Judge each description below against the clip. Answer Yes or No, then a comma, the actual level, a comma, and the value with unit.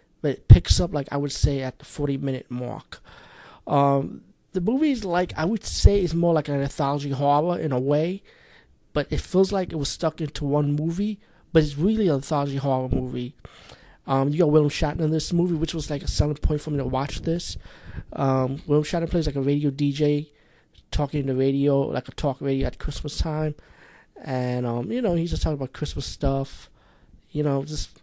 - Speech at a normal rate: No, fast, 210 wpm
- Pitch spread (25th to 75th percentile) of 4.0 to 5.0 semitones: No, average, 2.9 semitones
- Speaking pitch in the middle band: Yes, medium, 145 Hz